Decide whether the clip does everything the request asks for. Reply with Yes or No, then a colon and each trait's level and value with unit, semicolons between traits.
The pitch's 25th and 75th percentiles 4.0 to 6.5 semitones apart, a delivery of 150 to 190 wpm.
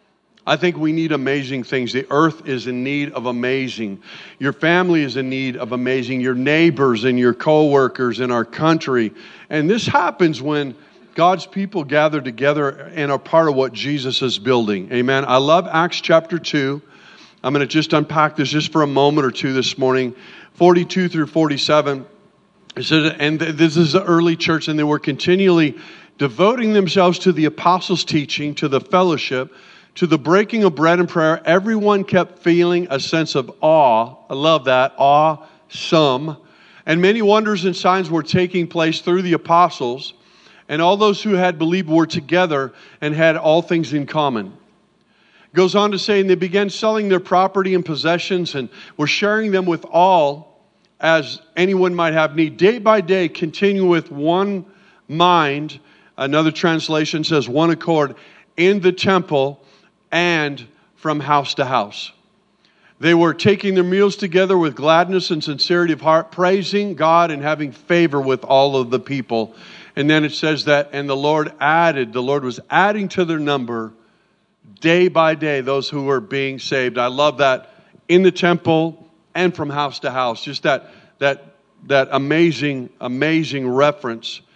Yes: average, 4.3 semitones; average, 170 wpm